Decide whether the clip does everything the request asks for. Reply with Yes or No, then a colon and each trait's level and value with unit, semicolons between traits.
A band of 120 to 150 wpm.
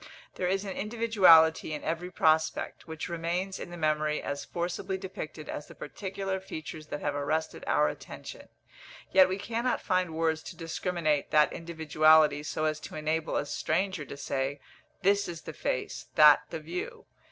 No: average, 165 wpm